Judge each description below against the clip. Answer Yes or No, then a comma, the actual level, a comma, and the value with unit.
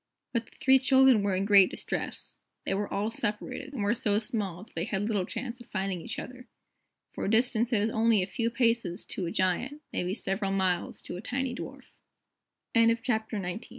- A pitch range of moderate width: Yes, average, 3.7 semitones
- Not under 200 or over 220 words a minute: No, average, 185 wpm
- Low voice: No, high, 220 Hz